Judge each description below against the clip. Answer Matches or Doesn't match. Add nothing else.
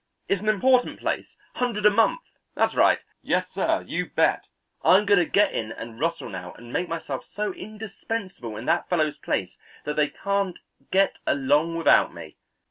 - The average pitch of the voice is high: Doesn't match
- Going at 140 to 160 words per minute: Doesn't match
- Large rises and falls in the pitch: Matches